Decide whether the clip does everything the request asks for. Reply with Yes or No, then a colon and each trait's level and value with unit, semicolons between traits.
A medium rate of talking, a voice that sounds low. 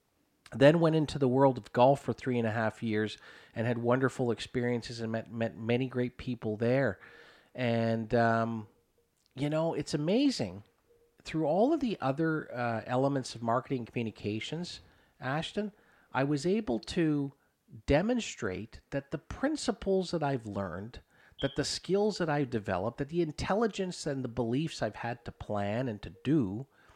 Yes: average, 160 wpm; low, 130 Hz